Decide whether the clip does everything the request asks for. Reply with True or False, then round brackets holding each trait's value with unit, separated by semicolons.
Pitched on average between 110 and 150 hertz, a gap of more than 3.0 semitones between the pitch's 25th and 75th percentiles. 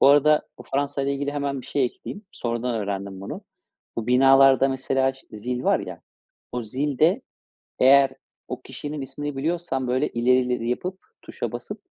False (135 Hz; 2.5 semitones)